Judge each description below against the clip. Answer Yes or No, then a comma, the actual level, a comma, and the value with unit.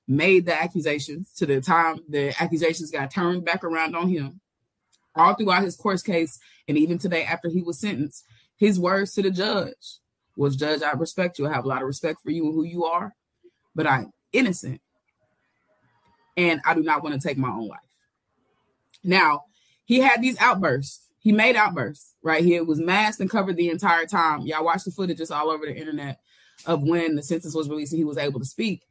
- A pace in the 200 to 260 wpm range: Yes, fast, 205 wpm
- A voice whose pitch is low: No, medium, 165 Hz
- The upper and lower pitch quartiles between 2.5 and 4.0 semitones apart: Yes, average, 3.6 semitones